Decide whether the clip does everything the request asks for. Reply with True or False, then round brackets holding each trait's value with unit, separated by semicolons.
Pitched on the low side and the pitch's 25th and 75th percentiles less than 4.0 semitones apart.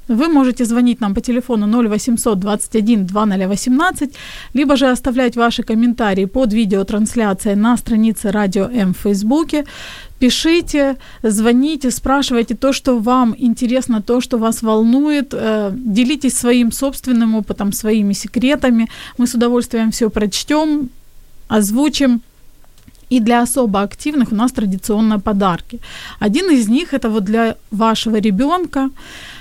False (235 Hz; 3.1 semitones)